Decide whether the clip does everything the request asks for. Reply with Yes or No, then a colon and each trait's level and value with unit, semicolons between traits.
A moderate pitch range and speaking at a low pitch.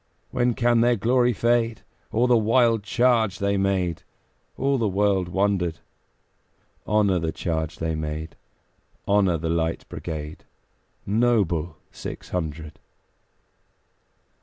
No: wide, 5.9 semitones; low, 100 Hz